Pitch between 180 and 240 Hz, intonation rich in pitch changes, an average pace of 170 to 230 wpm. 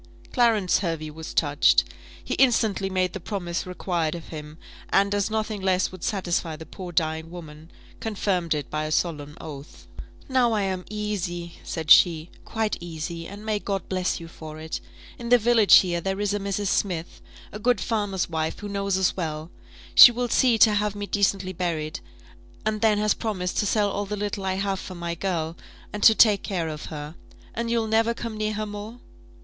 No: high, 190 Hz; average, 4.0 semitones; average, 195 wpm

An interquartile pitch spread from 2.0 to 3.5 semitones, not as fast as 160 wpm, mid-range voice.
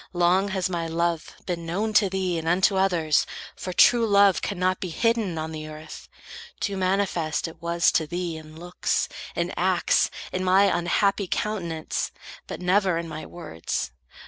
No: average, 2.7 semitones; average, 165 wpm; medium, 180 Hz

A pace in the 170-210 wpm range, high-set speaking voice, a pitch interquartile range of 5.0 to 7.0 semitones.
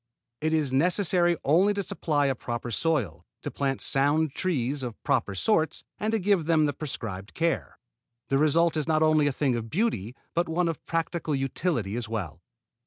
No: average, 180 wpm; medium, 150 Hz; average, 5.3 semitones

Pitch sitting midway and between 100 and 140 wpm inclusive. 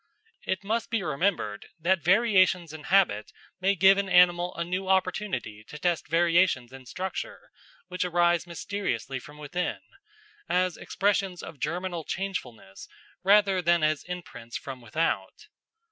Yes: medium, 175 Hz; slow, 135 wpm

